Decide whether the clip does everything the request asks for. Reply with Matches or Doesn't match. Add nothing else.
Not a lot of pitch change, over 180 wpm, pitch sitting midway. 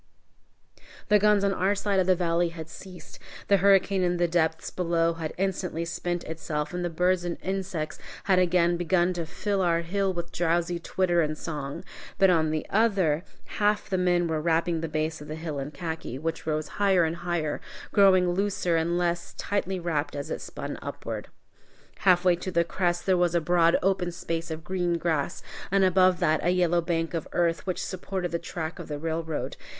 Matches